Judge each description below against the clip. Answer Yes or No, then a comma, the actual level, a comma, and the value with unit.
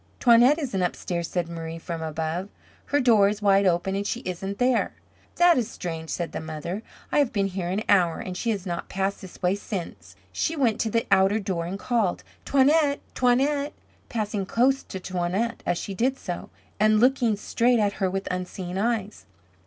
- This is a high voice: Yes, high, 200 Hz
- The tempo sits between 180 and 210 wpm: Yes, average, 190 wpm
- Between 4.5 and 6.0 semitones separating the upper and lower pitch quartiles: Yes, average, 4.8 semitones